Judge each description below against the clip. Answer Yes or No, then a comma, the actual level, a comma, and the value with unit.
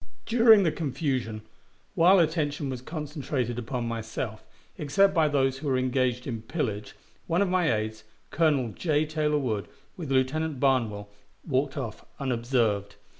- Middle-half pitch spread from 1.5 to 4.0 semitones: No, average, 4.9 semitones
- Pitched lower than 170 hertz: Yes, low, 135 Hz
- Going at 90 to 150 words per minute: Yes, average, 140 wpm